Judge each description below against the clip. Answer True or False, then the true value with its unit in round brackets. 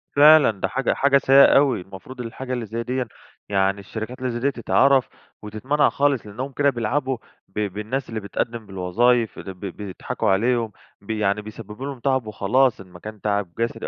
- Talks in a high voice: False (115 Hz)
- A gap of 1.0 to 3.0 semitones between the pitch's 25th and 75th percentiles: False (4.4 semitones)